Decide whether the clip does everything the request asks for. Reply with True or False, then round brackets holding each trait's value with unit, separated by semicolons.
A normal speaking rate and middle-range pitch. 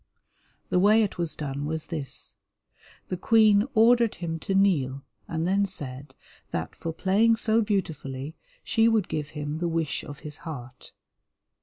True (155 wpm; 165 Hz)